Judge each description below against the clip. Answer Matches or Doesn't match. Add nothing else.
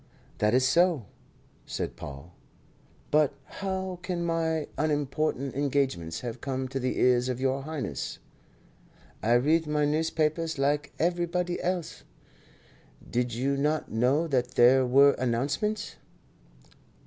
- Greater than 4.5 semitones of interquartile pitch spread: Doesn't match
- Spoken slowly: Matches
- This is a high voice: Doesn't match